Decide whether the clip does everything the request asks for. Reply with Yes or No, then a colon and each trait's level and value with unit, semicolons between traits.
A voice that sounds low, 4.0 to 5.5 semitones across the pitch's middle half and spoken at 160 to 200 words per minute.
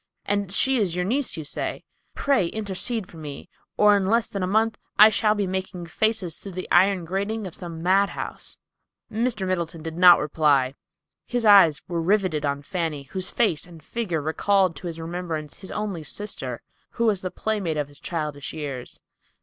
No: medium, 185 Hz; average, 4.3 semitones; average, 180 wpm